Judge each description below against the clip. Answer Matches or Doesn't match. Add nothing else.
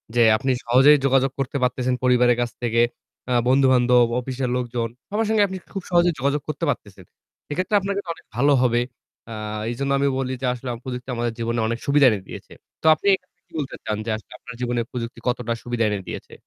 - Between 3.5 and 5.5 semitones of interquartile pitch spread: Doesn't match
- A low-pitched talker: Matches